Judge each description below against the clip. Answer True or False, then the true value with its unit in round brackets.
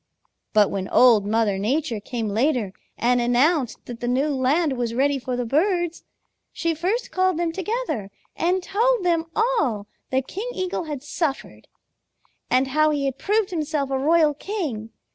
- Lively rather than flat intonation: True (6.1 semitones)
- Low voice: False (285 Hz)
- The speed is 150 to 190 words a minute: True (160 wpm)